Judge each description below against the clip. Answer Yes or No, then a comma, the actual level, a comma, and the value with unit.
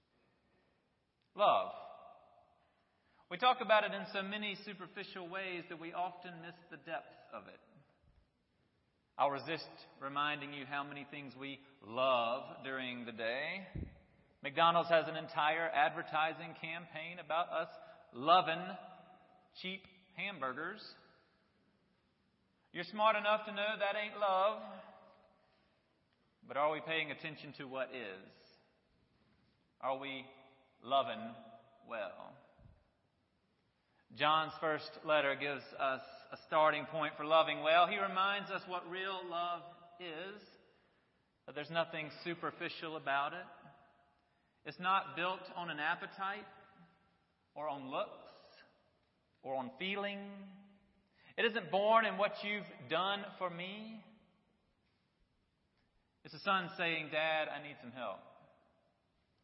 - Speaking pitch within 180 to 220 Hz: No, medium, 170 Hz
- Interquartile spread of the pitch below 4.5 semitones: No, average, 5.3 semitones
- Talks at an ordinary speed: No, slow, 115 wpm